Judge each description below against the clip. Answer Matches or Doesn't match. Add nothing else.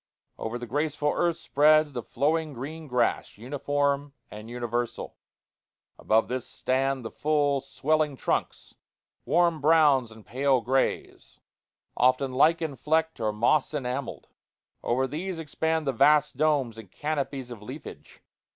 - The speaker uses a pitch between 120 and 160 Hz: Matches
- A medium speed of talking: Doesn't match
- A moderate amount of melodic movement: Matches